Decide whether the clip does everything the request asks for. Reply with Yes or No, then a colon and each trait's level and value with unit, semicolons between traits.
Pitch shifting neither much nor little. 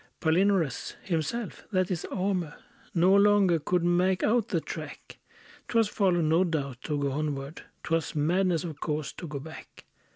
Yes: average, 3.7 semitones